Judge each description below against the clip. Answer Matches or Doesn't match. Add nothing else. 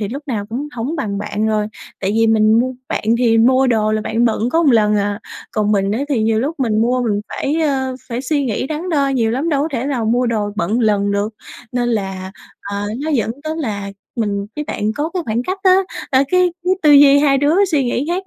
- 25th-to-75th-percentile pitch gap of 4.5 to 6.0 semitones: Matches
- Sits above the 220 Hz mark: Matches